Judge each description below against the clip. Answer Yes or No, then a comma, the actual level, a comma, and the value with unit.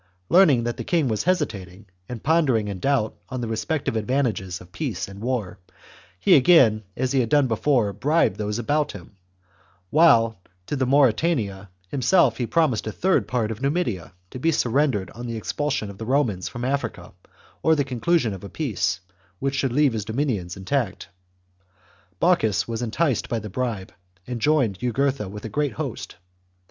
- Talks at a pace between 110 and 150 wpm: No, average, 175 wpm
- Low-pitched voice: Yes, low, 120 Hz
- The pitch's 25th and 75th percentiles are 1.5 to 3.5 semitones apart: No, average, 5.1 semitones